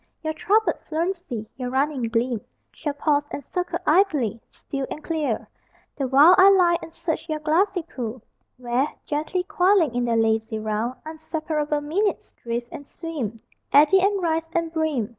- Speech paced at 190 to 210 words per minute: No, average, 160 wpm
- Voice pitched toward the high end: Yes, very high, 300 Hz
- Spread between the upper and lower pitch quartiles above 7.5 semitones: No, wide, 5.4 semitones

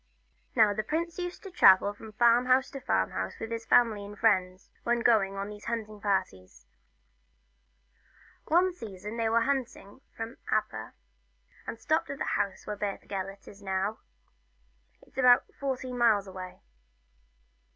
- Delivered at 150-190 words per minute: Yes, average, 155 wpm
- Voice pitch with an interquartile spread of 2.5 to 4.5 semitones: Yes, average, 3.8 semitones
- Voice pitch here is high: Yes, high, 220 Hz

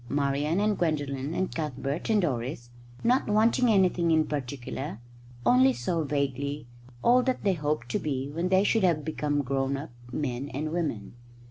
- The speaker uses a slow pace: No, average, 160 wpm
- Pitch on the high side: No, medium, 150 Hz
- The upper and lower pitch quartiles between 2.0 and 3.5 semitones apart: No, average, 4.5 semitones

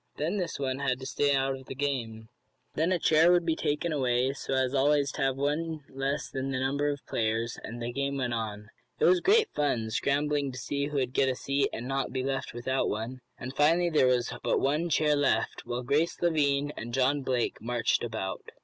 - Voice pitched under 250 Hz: Yes, low, 135 Hz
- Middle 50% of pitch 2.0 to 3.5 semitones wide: Yes, narrow, 2.6 semitones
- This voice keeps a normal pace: No, fast, 220 wpm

